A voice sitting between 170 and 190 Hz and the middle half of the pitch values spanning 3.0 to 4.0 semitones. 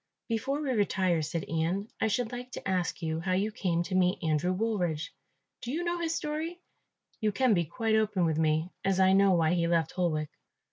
No: medium, 185 Hz; average, 5.0 semitones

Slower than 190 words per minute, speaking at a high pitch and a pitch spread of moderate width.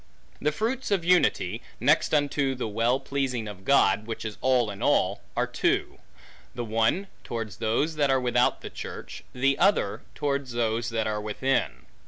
No: average, 170 wpm; low, 125 Hz; average, 4.1 semitones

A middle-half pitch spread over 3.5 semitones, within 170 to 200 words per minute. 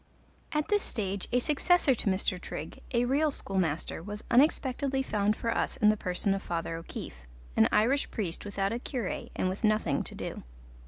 Yes: wide, 5.6 semitones; average, 180 wpm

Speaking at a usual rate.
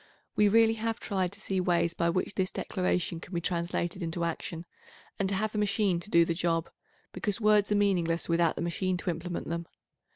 No: fast, 215 wpm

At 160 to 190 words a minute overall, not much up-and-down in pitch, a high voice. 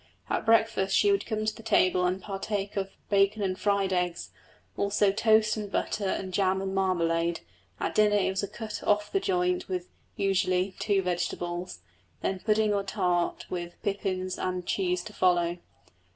Yes: average, 170 wpm; narrow, 2.3 semitones; high, 195 Hz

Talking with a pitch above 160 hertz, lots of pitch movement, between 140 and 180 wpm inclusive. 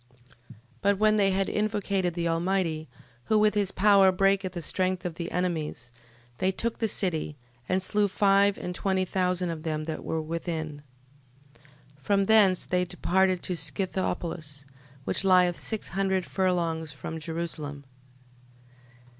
No: medium, 185 Hz; average, 2.9 semitones; average, 145 wpm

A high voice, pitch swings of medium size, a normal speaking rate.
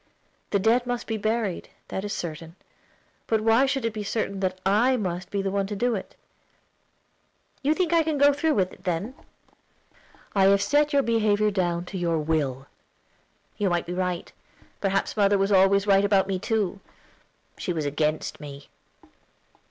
Yes: high, 200 Hz; average, 3.7 semitones; average, 175 wpm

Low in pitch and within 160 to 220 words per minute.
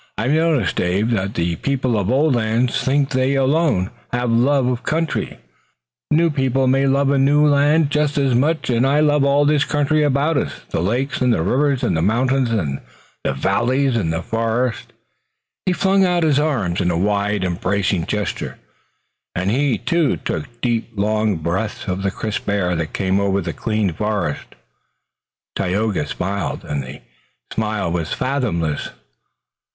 Yes: low, 120 Hz; average, 165 wpm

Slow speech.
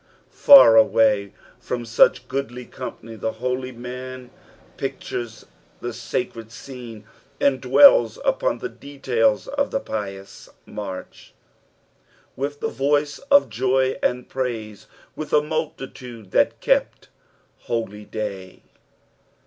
Yes: slow, 110 wpm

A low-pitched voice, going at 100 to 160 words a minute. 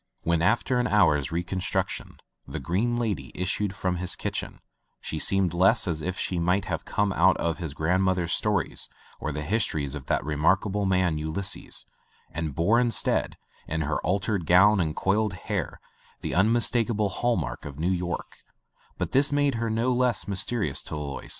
No: very low, 95 Hz; average, 175 wpm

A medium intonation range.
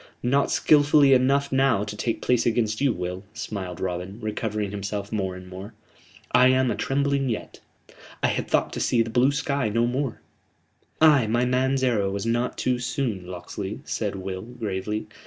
Yes: average, 4.5 semitones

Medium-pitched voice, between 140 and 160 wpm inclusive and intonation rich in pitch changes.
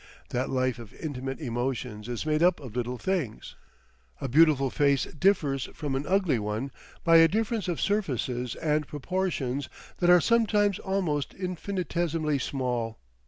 Yes: medium, 145 Hz; average, 145 wpm; wide, 5.9 semitones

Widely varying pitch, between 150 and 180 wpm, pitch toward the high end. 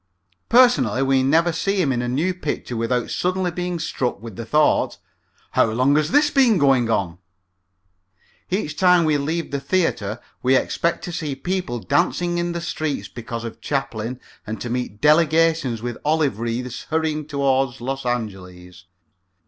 No: wide, 5.8 semitones; average, 160 wpm; medium, 140 Hz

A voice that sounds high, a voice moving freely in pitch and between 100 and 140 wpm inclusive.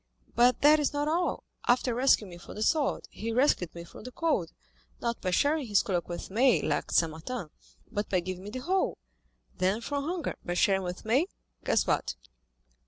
No: high, 230 Hz; wide, 7.4 semitones; average, 185 wpm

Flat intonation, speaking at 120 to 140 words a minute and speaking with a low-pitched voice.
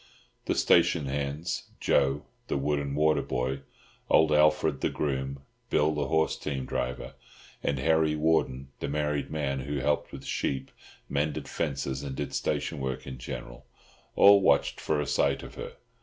No: narrow, 2.2 semitones; average, 155 wpm; very low, 70 Hz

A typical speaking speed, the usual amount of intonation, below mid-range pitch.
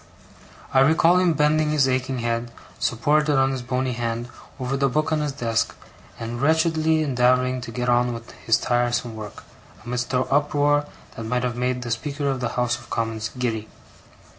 Yes: average, 180 wpm; average, 3.3 semitones; low, 125 Hz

